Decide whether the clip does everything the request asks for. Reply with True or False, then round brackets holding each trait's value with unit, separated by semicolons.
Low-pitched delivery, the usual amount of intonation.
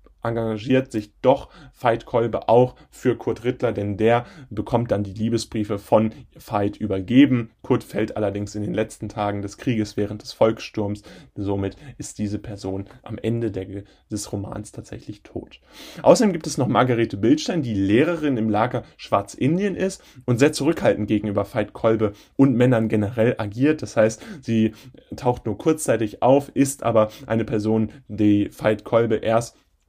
True (110 Hz; 3.7 semitones)